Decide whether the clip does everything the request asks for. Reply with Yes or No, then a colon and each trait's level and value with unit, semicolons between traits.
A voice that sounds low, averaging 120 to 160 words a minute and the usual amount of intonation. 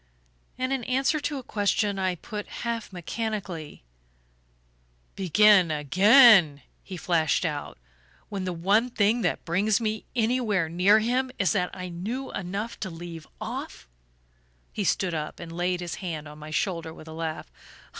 No: high, 190 Hz; average, 155 wpm; average, 4.6 semitones